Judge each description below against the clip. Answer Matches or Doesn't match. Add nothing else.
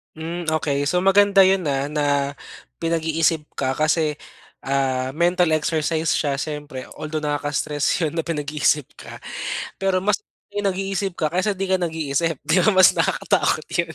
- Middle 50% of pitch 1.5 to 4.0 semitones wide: Matches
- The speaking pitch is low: Doesn't match